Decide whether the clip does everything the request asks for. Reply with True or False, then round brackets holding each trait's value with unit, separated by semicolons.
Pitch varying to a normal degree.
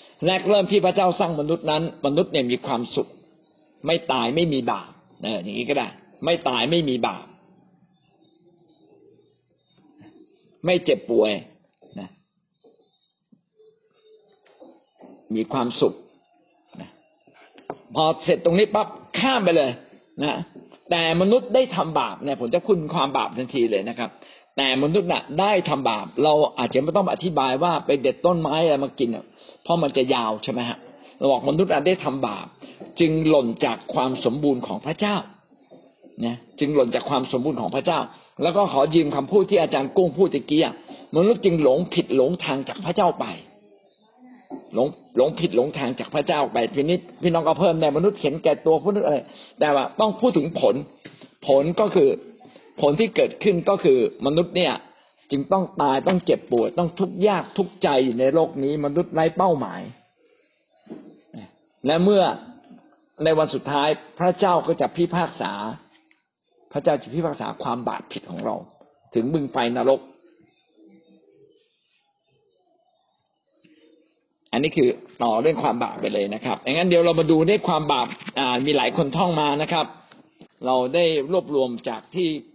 False (6.2 semitones)